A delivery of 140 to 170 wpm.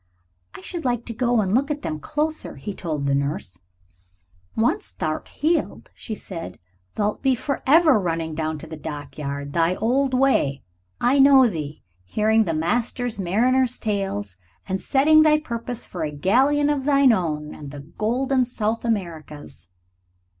Yes: average, 155 wpm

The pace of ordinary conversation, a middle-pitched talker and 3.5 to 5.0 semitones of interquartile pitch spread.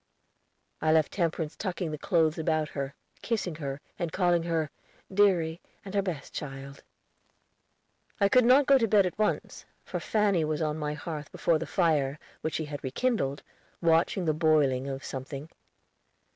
Yes: average, 160 wpm; medium, 160 Hz; average, 3.8 semitones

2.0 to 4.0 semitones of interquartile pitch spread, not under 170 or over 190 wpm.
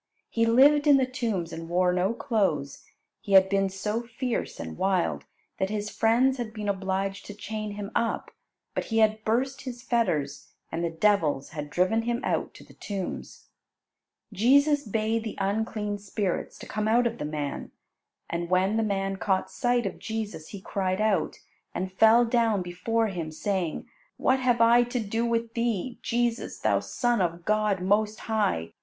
Yes: average, 3.6 semitones; average, 175 wpm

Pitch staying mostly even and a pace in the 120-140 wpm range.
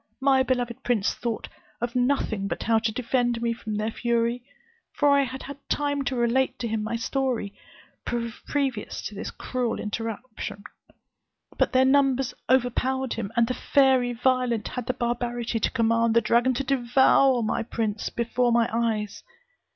No: narrow, 2.2 semitones; average, 160 wpm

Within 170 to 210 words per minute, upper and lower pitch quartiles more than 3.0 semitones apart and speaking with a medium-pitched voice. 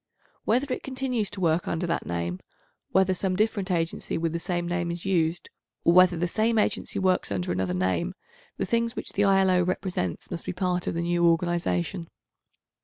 No: average, 185 wpm; narrow, 2.5 semitones; medium, 175 Hz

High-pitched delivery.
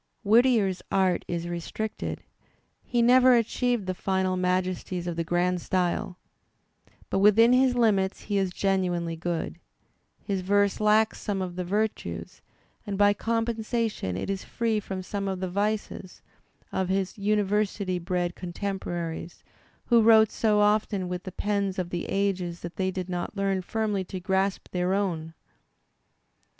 Yes: high, 195 Hz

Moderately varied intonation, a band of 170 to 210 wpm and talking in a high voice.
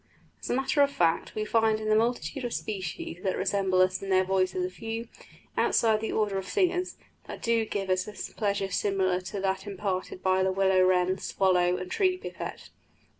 Yes: average, 3.1 semitones; average, 200 wpm; high, 195 Hz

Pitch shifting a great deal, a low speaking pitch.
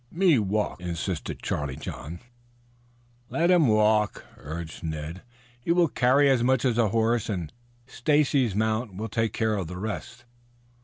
Yes: wide, 5.7 semitones; low, 110 Hz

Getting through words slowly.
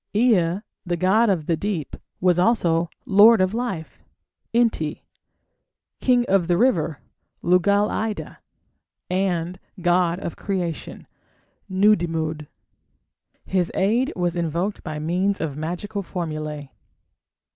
Yes: slow, 110 wpm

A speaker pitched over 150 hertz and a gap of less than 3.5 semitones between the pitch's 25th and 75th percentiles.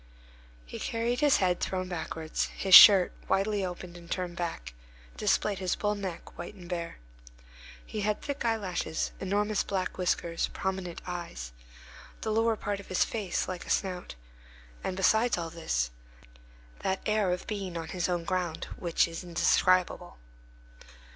Yes: medium, 185 Hz; average, 2.9 semitones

